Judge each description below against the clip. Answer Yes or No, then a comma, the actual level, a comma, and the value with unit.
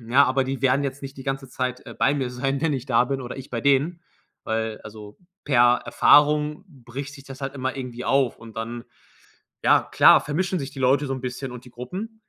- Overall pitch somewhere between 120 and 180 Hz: Yes, low, 135 Hz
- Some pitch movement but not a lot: No, narrow, 2.3 semitones